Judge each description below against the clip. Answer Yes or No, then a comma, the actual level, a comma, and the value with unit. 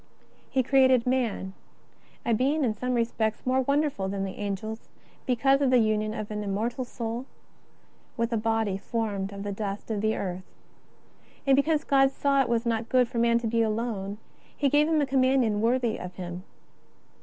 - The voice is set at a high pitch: Yes, high, 230 Hz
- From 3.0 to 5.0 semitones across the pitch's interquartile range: Yes, average, 3.6 semitones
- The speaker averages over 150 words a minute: Yes, average, 190 wpm